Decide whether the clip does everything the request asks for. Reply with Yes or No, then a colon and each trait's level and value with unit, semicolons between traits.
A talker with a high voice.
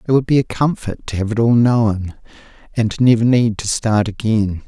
No: low, 110 Hz